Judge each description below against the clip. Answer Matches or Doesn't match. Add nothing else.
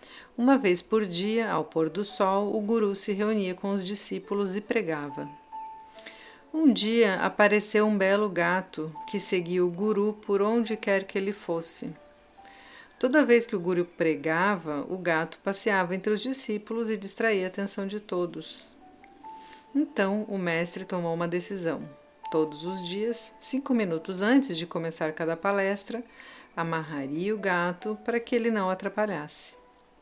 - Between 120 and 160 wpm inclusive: Matches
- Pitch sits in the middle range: Doesn't match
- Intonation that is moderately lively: Matches